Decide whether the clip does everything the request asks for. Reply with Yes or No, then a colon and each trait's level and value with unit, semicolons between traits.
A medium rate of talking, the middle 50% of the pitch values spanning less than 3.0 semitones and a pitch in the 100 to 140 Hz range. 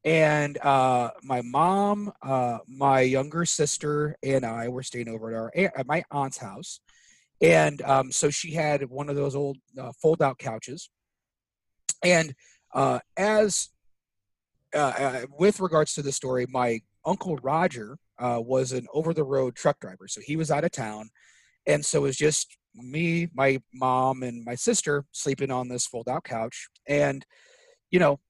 No: average, 165 wpm; average, 3.7 semitones; low, 135 Hz